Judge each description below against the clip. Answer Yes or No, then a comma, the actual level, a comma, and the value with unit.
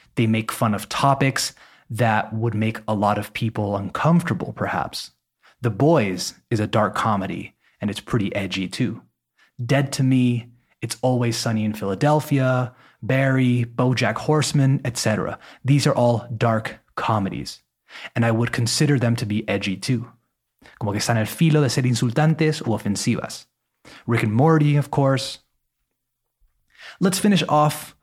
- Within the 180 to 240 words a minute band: No, average, 150 wpm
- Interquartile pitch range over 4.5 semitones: No, average, 4.0 semitones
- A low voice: Yes, low, 120 Hz